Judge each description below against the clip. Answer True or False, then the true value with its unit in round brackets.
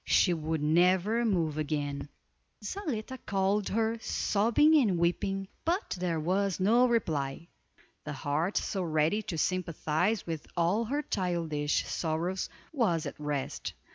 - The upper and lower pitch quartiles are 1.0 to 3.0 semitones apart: False (5.3 semitones)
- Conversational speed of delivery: False (130 wpm)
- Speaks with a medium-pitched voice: True (180 Hz)